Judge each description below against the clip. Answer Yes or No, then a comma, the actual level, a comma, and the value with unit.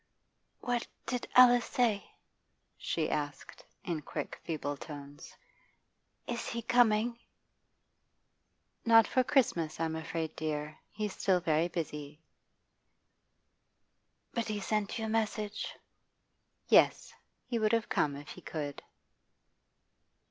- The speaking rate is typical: No, slow, 110 wpm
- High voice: Yes, high, 200 Hz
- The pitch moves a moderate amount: No, wide, 6.9 semitones